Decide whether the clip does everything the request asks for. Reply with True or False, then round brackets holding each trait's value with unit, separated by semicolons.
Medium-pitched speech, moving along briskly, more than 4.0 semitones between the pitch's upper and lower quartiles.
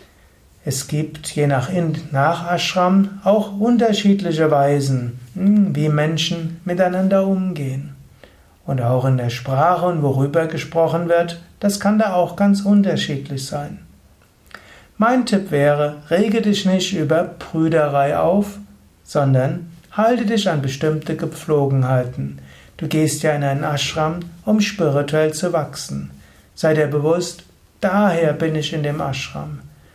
False (160 Hz; 130 wpm; 4.6 semitones)